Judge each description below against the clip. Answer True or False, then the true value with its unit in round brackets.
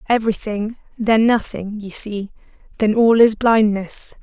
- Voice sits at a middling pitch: False (220 Hz)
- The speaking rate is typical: False (130 wpm)